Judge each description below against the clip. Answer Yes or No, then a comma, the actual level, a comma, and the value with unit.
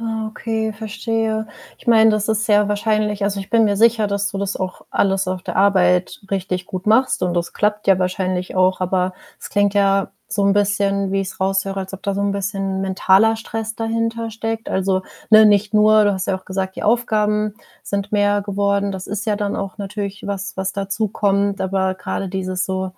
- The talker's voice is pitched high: Yes, high, 200 Hz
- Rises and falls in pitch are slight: Yes, narrow, 1.9 semitones